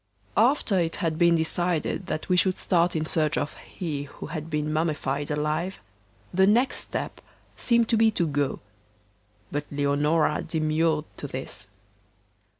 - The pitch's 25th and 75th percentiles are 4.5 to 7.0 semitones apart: No, average, 3.3 semitones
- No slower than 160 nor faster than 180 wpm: No, average, 150 wpm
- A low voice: No, medium, 160 Hz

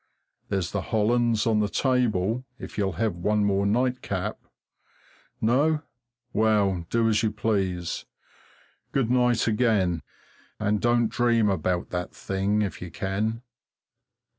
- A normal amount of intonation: Yes, average, 3.3 semitones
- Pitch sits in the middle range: No, low, 105 Hz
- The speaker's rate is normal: No, slow, 125 wpm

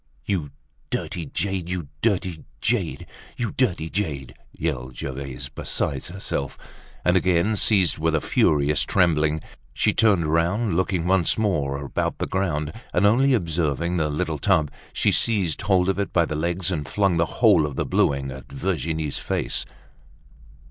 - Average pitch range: Yes, average, 4.3 semitones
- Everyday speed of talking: Yes, average, 155 wpm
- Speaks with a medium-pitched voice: No, very low, 85 Hz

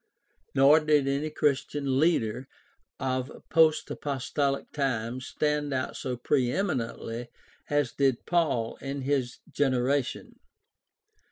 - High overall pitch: No, low, 135 Hz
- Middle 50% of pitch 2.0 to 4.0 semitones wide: Yes, narrow, 2.5 semitones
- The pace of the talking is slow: Yes, slow, 105 wpm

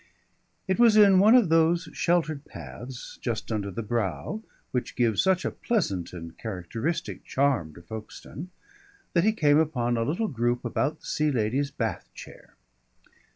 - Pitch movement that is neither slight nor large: No, wide, 7.5 semitones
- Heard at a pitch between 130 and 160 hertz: Yes, low, 135 Hz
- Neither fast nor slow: Yes, average, 155 wpm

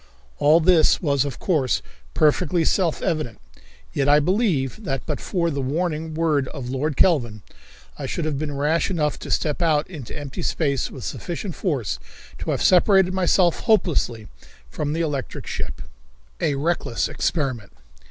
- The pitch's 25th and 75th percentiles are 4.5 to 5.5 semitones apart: No, average, 3.8 semitones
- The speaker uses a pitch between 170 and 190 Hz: No, medium, 150 Hz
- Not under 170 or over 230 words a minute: No, average, 155 wpm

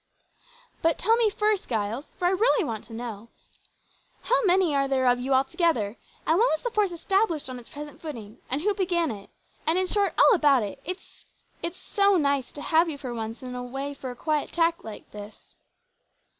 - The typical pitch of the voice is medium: No, very high, 295 Hz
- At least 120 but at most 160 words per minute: No, average, 200 wpm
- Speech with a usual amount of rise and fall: No, wide, 6.8 semitones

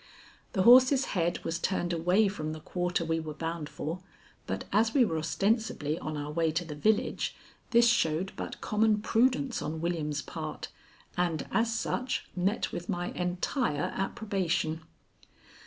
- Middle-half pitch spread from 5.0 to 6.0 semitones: Yes, average, 5.3 semitones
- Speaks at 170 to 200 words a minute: No, average, 155 wpm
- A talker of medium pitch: Yes, medium, 180 Hz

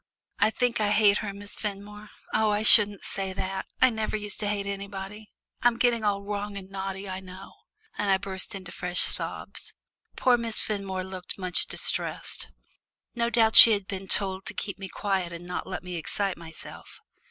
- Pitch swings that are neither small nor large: No, narrow, 1.8 semitones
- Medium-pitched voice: No, high, 200 Hz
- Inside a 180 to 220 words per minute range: Yes, average, 185 wpm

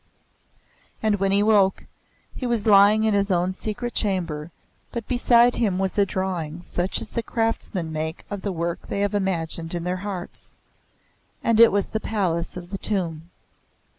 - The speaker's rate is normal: Yes, average, 170 wpm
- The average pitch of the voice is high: Yes, high, 195 Hz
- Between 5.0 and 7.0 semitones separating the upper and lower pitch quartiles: No, average, 3.6 semitones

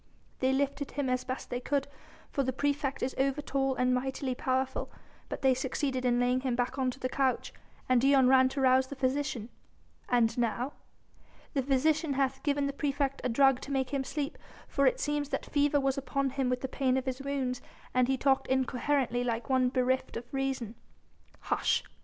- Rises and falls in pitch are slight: Yes, narrow, 1.6 semitones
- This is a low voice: No, very high, 265 Hz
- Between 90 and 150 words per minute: No, average, 195 wpm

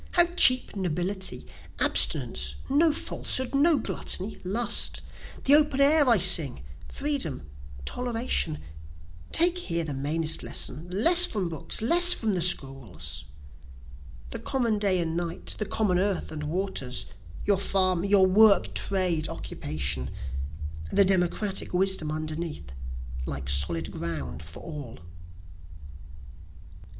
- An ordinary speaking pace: No, slow, 120 wpm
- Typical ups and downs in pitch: No, wide, 6.7 semitones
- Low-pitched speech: No, medium, 185 Hz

